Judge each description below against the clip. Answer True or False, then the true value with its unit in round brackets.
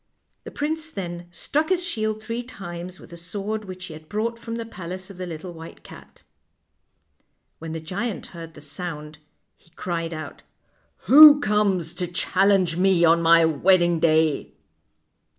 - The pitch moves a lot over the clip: False (4.3 semitones)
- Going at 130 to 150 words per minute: False (165 wpm)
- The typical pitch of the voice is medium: True (180 Hz)